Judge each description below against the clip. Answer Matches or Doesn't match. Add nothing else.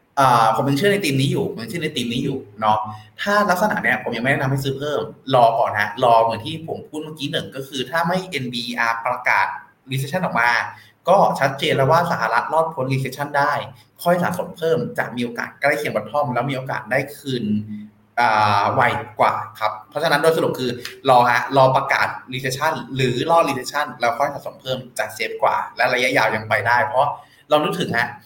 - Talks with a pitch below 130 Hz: Doesn't match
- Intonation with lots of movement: Doesn't match